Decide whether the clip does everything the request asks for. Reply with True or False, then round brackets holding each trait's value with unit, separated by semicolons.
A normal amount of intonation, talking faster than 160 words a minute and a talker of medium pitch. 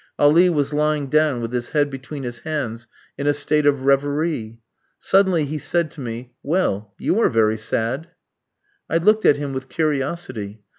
True (4.2 semitones; 170 wpm; 145 Hz)